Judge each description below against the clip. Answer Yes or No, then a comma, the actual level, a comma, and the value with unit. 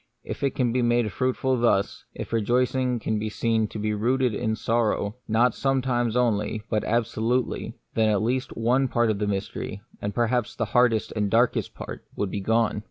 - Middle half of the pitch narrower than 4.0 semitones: Yes, narrow, 2.6 semitones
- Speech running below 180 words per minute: No, average, 195 wpm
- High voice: No, low, 115 Hz